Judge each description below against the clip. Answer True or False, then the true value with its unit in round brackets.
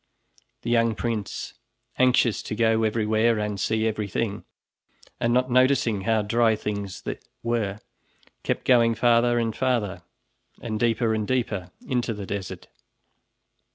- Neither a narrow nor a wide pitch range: False (2.1 semitones)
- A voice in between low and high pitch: False (115 Hz)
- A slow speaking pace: True (125 wpm)